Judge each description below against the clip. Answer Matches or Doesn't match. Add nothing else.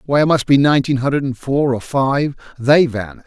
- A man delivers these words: Matches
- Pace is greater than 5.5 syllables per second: Matches